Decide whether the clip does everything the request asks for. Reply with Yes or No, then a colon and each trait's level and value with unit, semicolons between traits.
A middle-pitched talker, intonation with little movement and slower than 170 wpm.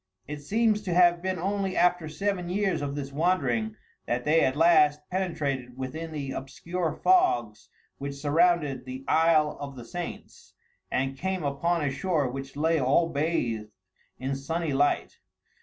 No: medium, 150 Hz; average, 4.3 semitones; average, 155 wpm